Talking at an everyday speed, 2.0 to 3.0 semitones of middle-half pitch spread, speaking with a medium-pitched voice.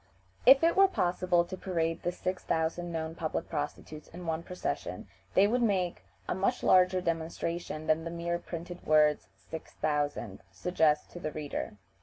Yes: average, 165 wpm; narrow, 2.6 semitones; medium, 170 Hz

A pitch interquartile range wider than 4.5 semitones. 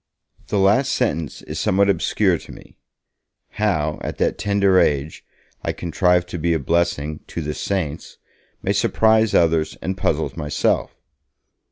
No: average, 4.2 semitones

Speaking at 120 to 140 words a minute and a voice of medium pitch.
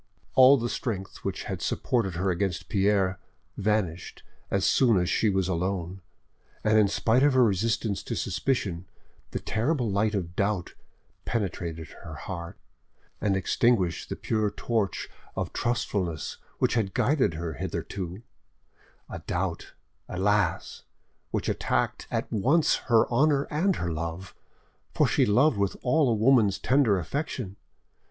No: slow, 135 wpm; low, 100 Hz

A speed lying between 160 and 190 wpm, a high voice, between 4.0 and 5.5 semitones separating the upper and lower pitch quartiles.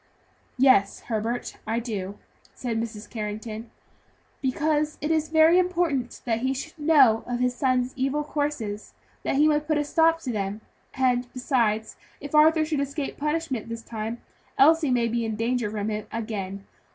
Yes: average, 165 wpm; very high, 250 Hz; average, 5.1 semitones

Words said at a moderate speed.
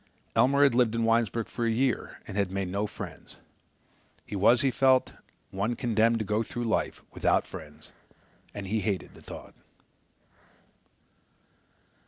Yes: average, 150 wpm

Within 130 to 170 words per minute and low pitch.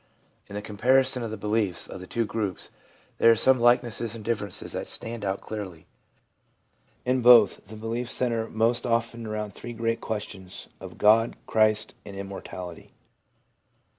Yes: average, 165 wpm; low, 110 Hz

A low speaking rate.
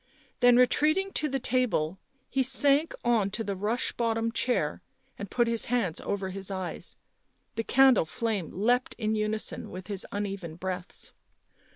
No: average, 155 wpm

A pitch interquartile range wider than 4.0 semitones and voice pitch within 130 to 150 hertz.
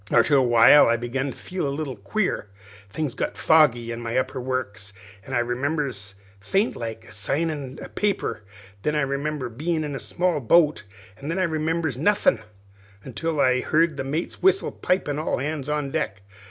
Yes: average, 4.6 semitones; medium, 140 Hz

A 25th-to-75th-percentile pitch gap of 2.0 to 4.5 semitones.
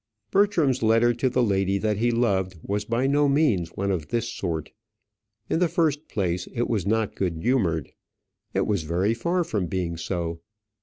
No: wide, 5.6 semitones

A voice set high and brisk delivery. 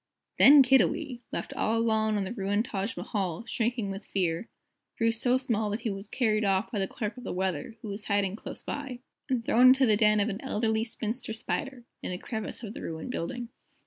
Yes: high, 220 Hz; fast, 210 wpm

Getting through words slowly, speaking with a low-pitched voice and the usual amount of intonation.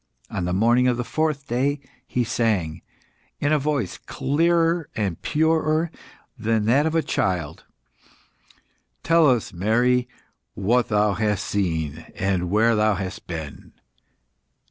No: slow, 125 wpm; low, 115 Hz; wide, 6.6 semitones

